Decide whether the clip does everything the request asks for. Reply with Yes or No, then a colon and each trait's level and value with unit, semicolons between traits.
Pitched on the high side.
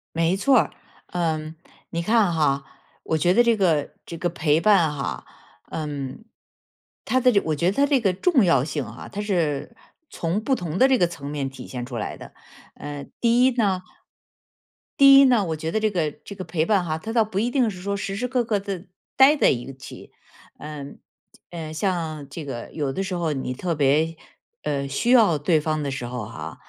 No: medium, 170 Hz